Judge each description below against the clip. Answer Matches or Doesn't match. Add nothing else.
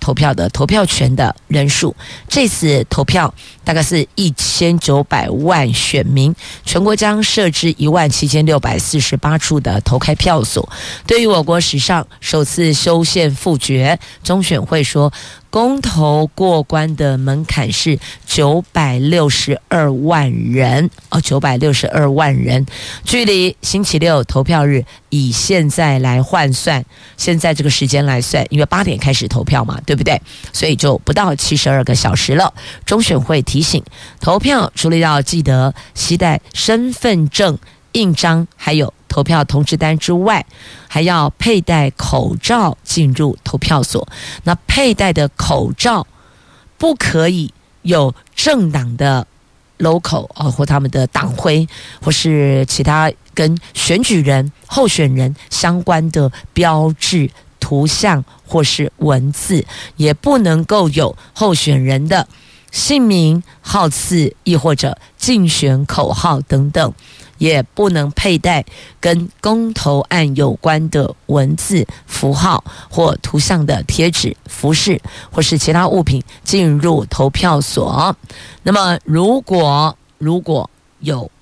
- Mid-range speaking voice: Matches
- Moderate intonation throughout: Matches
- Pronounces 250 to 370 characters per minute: Doesn't match